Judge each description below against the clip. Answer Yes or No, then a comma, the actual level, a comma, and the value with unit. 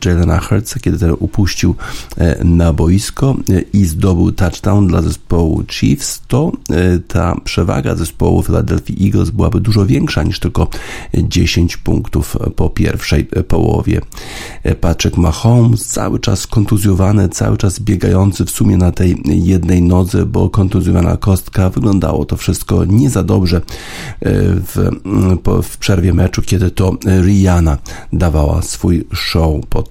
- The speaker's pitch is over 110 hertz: No, very low, 95 Hz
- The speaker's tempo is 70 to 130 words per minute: Yes, average, 125 wpm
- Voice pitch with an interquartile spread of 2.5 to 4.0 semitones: Yes, average, 3.2 semitones